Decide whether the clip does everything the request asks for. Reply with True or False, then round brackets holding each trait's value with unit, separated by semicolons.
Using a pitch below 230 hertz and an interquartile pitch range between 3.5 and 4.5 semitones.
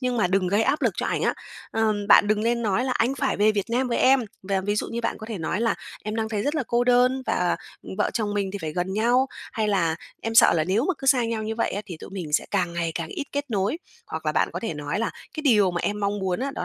True (215 Hz; 4.1 semitones)